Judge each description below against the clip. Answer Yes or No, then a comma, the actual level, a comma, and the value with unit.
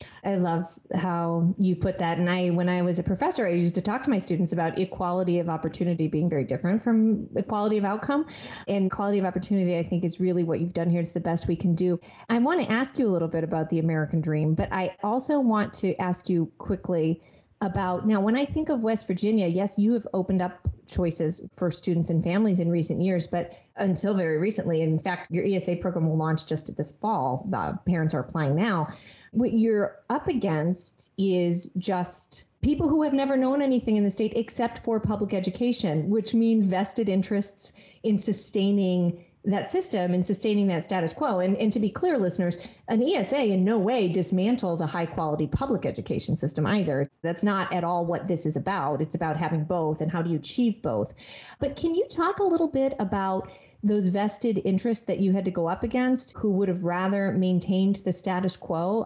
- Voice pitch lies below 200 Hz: Yes, medium, 185 Hz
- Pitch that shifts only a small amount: No, average, 3.4 semitones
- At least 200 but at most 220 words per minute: Yes, fast, 205 wpm